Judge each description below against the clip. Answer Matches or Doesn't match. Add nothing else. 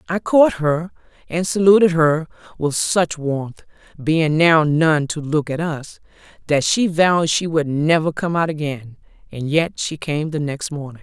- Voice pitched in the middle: Matches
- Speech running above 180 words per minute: Doesn't match